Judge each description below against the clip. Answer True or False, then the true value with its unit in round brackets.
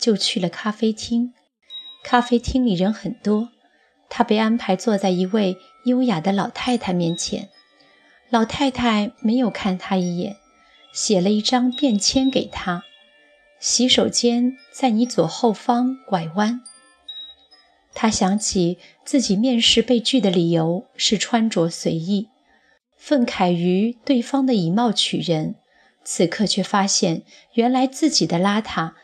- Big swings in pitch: False (4.6 semitones)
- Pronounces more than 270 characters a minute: False (195 characters per minute)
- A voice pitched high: True (220 Hz)